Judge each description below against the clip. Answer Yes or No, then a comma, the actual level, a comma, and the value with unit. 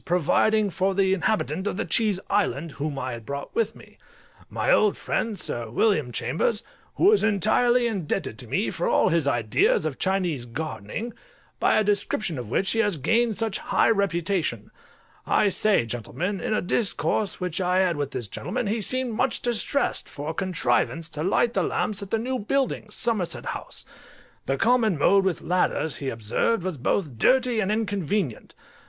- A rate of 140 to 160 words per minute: No, average, 175 wpm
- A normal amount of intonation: No, wide, 6.2 semitones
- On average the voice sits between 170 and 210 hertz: Yes, high, 190 Hz